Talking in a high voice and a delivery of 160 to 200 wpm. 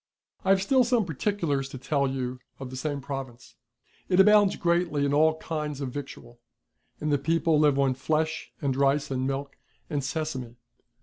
No: medium, 145 Hz; average, 175 wpm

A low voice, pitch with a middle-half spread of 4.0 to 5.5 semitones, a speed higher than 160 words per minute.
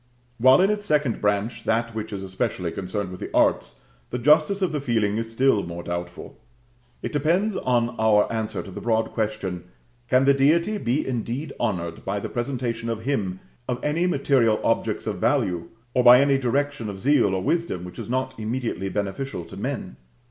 Yes: low, 115 Hz; average, 5.2 semitones; average, 185 wpm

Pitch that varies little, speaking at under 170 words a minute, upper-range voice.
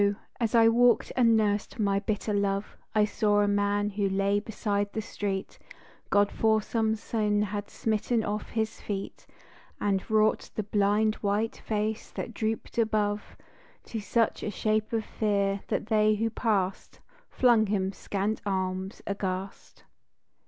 Yes: narrow, 1.4 semitones; average, 145 wpm; high, 210 Hz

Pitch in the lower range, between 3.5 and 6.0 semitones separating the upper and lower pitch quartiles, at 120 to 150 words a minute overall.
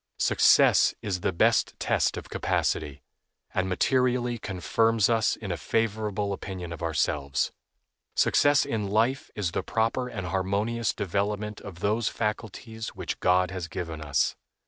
Yes: low, 100 Hz; average, 3.8 semitones; average, 140 wpm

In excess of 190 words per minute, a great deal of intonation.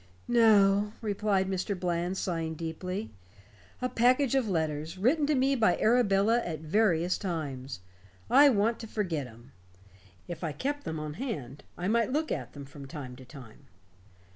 No: average, 160 wpm; wide, 6.4 semitones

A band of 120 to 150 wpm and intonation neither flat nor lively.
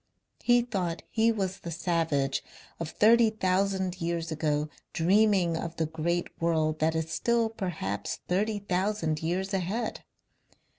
Yes: slow, 135 wpm; average, 4.0 semitones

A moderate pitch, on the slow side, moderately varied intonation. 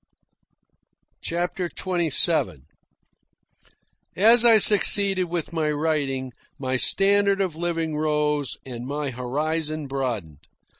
Yes: medium, 155 Hz; slow, 95 wpm; average, 4.9 semitones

